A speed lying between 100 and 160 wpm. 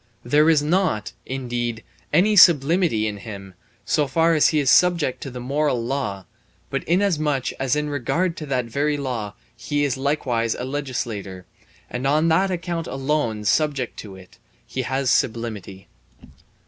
Yes: average, 155 wpm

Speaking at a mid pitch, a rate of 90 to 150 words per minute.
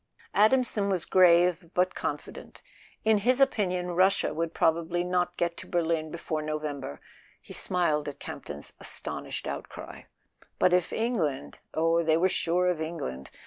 Yes: medium, 170 Hz; average, 145 wpm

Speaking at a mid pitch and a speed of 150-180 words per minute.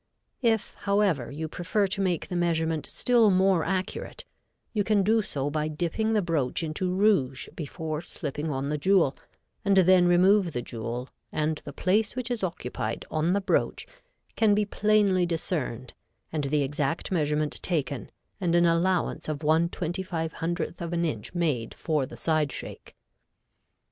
Yes: medium, 170 Hz; average, 155 wpm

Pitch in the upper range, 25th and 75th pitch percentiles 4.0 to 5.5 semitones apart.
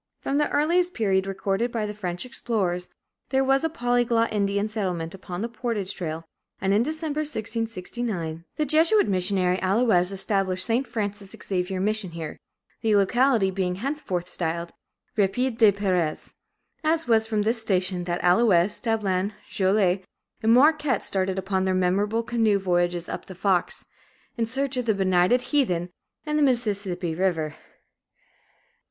Yes: high, 200 Hz; average, 4.5 semitones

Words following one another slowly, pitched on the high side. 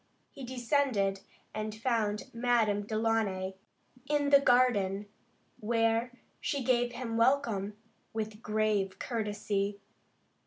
Yes: slow, 95 wpm; high, 225 Hz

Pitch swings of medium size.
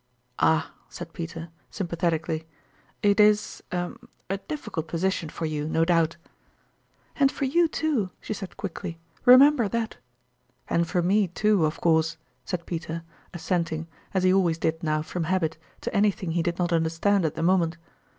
Yes: average, 3.6 semitones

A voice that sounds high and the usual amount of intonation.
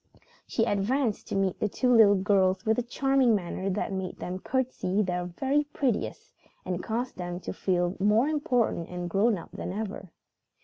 Yes: high, 205 Hz; average, 4.8 semitones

